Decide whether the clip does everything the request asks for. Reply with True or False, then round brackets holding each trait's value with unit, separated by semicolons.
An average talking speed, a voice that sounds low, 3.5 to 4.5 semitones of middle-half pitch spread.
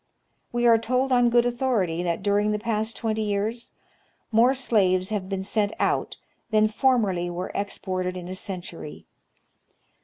False (155 wpm; 210 Hz; 4.1 semitones)